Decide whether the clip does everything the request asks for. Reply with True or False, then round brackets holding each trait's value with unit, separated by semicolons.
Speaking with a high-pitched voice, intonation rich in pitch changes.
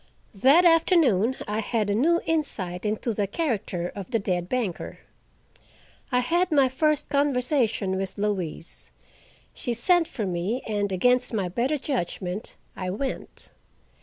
True (230 Hz; 6.3 semitones)